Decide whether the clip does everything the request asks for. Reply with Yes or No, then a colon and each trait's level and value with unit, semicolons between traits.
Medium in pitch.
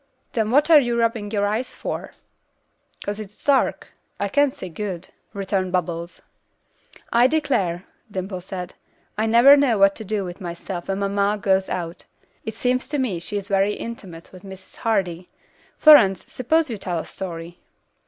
No: high, 200 Hz